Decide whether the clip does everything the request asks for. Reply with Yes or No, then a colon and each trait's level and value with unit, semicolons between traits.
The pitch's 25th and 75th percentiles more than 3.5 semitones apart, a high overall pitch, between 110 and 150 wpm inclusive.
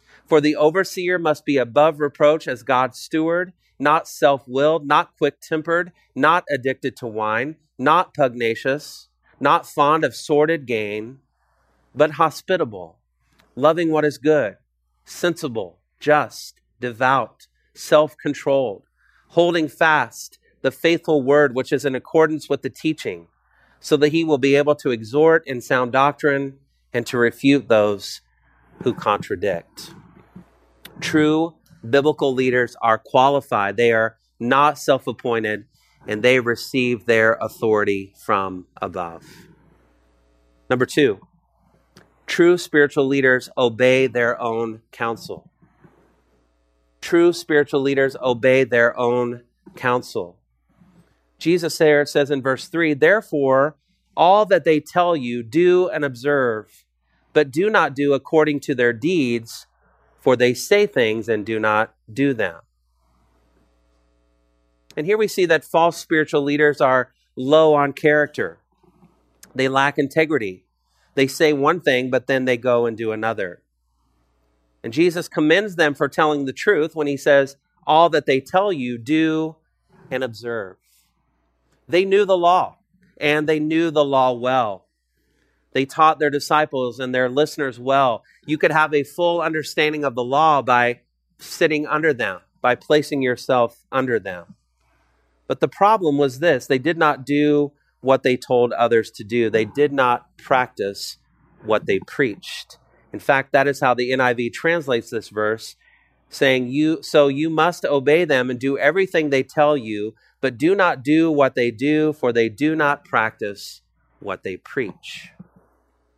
No: average, 4.9 semitones; low, 135 Hz; average, 140 wpm